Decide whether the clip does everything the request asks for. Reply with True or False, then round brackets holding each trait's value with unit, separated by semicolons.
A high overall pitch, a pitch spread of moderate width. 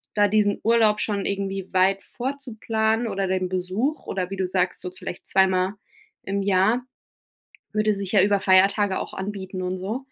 False (195 Hz; 2.3 semitones)